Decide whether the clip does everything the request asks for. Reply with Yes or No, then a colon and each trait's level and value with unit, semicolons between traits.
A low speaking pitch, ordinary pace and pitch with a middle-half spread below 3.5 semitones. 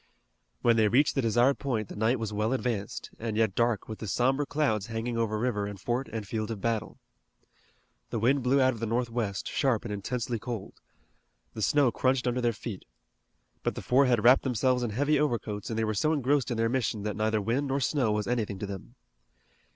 No: low, 115 Hz; fast, 215 wpm; average, 3.0 semitones